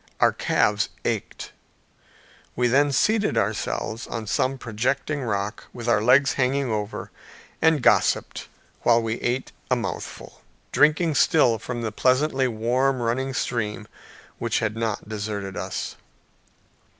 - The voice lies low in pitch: Yes, low, 120 Hz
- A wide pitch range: No, average, 3.6 semitones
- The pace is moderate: No, slow, 125 wpm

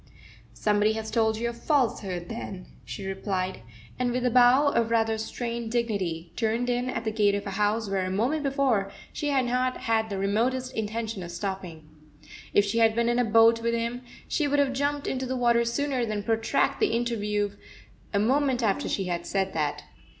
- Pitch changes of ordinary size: Yes, average, 3.3 semitones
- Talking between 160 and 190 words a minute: No, average, 200 wpm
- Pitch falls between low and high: No, high, 225 Hz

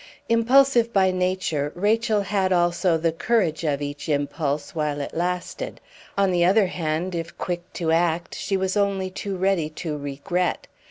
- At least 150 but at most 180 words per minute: Yes, average, 160 wpm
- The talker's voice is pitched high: No, medium, 180 Hz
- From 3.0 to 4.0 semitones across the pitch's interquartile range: Yes, average, 3.5 semitones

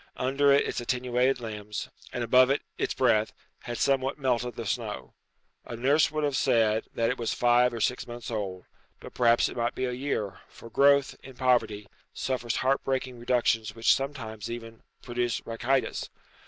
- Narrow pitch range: Yes, narrow, 2.3 semitones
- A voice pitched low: Yes, low, 120 Hz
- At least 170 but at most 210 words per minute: Yes, average, 175 wpm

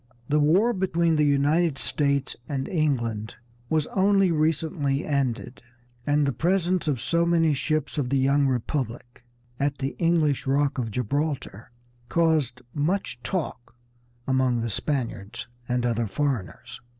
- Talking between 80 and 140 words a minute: Yes, slow, 135 wpm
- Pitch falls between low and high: Yes, medium, 145 Hz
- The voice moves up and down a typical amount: Yes, average, 4.0 semitones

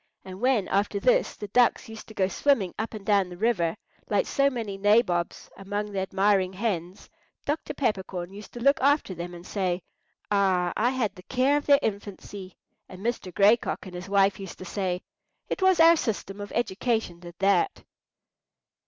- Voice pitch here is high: Yes, high, 200 Hz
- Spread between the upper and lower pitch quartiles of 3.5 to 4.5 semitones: Yes, average, 3.9 semitones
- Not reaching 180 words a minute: No, average, 185 wpm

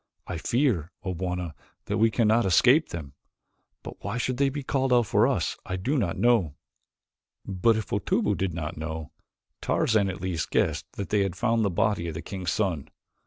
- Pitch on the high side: No, very low, 95 Hz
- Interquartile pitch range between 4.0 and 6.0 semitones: Yes, average, 5.3 semitones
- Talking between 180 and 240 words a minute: Yes, average, 190 wpm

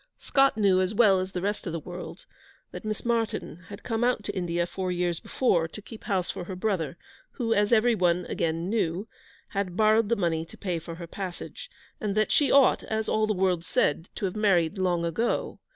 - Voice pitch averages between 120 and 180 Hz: No, high, 190 Hz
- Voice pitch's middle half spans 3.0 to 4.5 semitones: Yes, average, 3.8 semitones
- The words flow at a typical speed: No, fast, 215 wpm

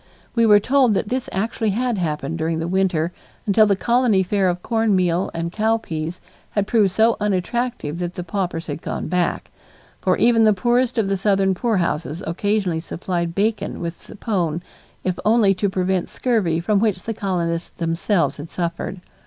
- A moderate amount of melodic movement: Yes, average, 4.2 semitones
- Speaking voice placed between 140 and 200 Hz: Yes, high, 190 Hz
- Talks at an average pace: Yes, average, 175 wpm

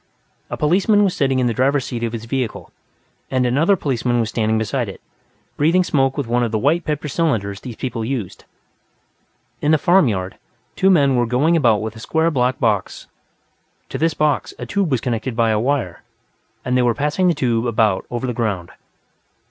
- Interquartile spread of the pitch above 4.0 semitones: Yes, average, 4.6 semitones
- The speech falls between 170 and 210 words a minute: Yes, average, 195 wpm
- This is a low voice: Yes, low, 125 Hz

